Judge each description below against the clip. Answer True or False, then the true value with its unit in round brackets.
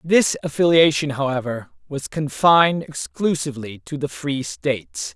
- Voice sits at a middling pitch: True (145 Hz)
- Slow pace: True (115 wpm)